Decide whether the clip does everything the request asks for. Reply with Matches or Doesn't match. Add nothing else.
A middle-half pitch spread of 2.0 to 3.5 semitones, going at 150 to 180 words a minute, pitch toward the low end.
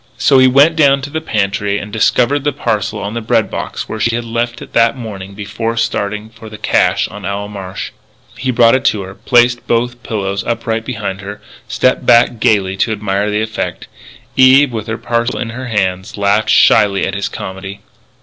Doesn't match